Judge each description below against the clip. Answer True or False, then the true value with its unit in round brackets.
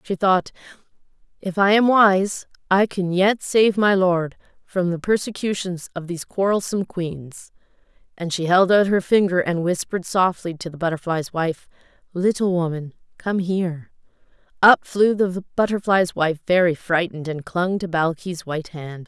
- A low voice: False (180 Hz)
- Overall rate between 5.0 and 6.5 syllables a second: False (4.7 syllables/s)